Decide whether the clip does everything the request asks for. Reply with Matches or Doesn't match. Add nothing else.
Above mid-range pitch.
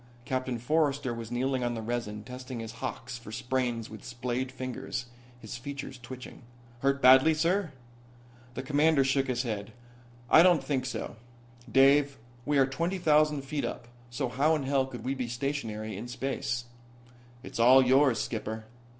Doesn't match